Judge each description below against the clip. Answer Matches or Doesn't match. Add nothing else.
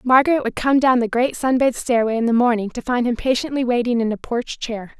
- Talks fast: Matches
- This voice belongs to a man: Doesn't match